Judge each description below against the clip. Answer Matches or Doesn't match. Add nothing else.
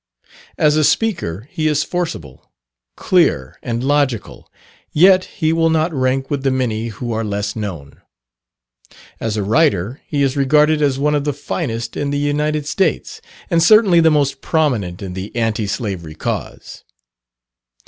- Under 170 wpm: Matches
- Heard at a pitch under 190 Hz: Matches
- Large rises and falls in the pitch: Matches